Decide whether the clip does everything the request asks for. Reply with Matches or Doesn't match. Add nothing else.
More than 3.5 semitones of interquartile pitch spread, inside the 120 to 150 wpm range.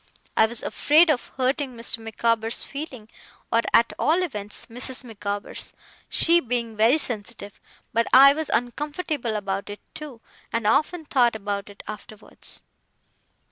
Matches